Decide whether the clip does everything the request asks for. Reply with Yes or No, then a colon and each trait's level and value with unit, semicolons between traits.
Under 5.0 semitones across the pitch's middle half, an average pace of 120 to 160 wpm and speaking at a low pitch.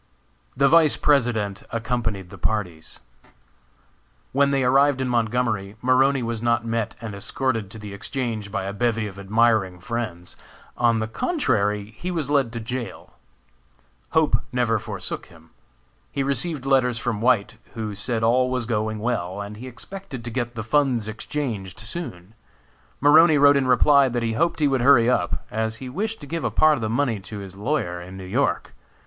No: average, 4.1 semitones; average, 175 wpm; low, 115 Hz